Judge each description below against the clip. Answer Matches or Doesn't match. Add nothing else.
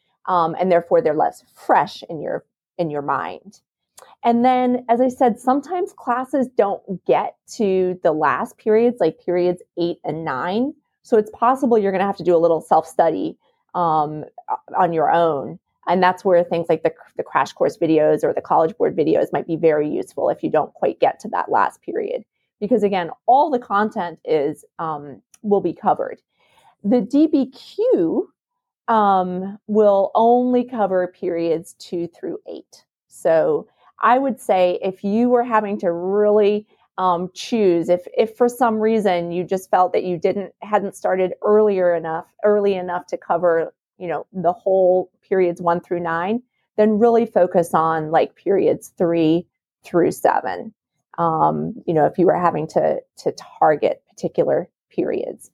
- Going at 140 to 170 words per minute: Matches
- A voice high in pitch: Matches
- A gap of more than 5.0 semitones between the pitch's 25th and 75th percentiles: Matches